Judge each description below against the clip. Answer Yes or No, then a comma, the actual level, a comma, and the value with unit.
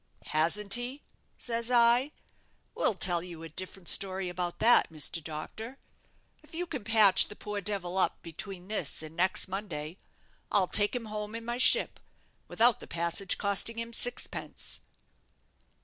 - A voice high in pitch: Yes, high, 200 Hz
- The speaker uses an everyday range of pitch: Yes, average, 4.6 semitones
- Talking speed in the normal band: Yes, average, 150 wpm